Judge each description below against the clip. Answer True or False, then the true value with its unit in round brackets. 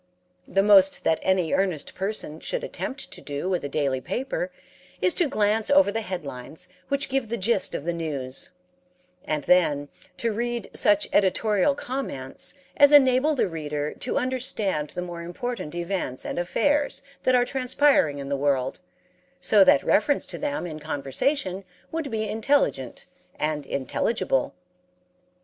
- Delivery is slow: False (150 wpm)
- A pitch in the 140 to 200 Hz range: True (190 Hz)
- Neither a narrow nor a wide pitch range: False (8.7 semitones)